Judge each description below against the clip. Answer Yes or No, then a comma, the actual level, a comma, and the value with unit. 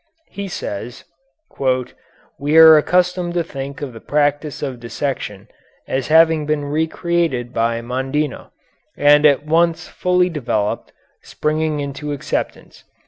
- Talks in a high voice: No, medium, 150 Hz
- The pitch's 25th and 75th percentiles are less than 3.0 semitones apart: No, average, 3.4 semitones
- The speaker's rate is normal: No, slow, 125 wpm